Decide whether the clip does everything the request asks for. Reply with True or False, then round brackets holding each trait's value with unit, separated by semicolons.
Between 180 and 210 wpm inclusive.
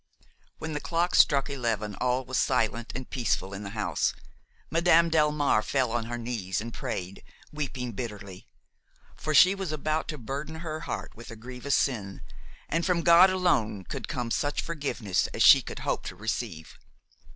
False (170 wpm)